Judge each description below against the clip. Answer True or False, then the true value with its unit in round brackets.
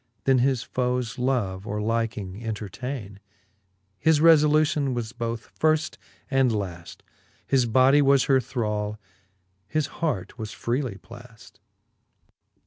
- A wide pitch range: False (4.0 semitones)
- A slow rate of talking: True (115 wpm)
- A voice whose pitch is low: True (120 Hz)